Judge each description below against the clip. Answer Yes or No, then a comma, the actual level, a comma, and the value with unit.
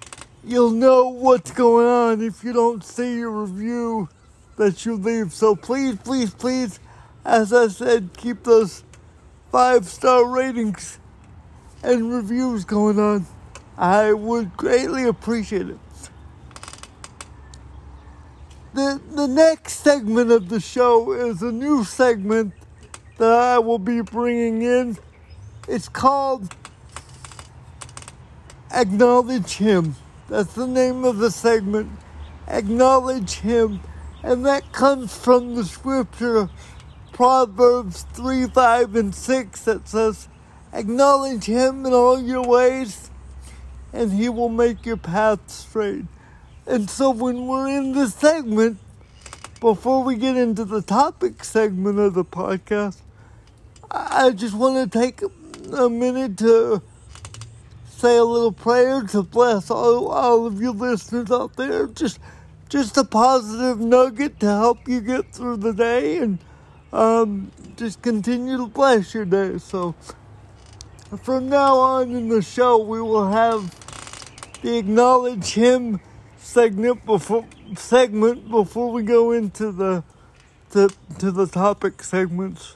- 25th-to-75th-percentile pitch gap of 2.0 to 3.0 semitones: No, average, 3.6 semitones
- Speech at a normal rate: No, slow, 125 wpm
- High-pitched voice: Yes, high, 230 Hz